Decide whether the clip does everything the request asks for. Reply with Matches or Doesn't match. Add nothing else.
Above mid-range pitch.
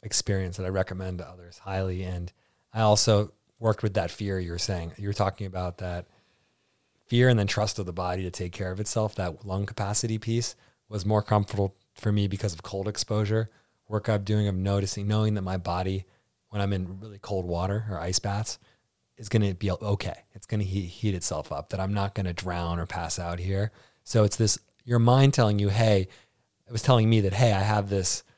Doesn't match